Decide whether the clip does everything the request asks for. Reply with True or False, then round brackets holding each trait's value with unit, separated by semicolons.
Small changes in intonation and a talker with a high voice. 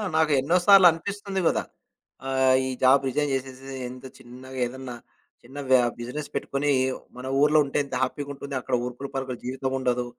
False (2.2 semitones; 135 Hz)